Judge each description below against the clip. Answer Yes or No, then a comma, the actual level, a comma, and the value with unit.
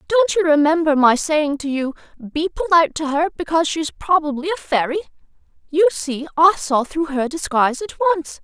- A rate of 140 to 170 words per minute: No, average, 180 wpm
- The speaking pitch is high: Yes, very high, 315 Hz